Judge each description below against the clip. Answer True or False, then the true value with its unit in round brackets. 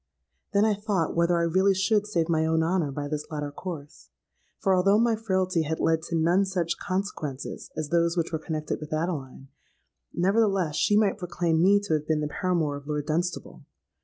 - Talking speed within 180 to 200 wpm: True (190 wpm)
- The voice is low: False (170 Hz)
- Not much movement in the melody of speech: False (3.6 semitones)